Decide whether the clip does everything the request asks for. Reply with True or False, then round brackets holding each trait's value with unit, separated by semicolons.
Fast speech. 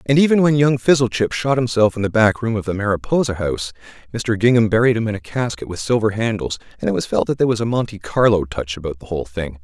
True (250 wpm)